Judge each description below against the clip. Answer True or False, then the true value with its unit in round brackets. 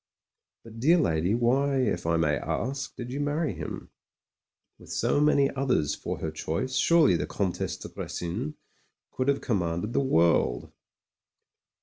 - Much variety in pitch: True (8.7 semitones)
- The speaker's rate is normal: True (145 wpm)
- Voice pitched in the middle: False (120 Hz)